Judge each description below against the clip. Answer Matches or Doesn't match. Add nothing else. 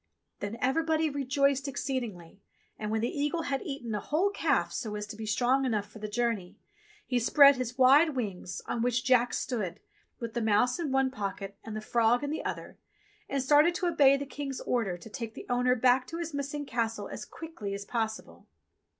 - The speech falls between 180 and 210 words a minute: Matches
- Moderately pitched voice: Doesn't match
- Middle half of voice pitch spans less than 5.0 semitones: Matches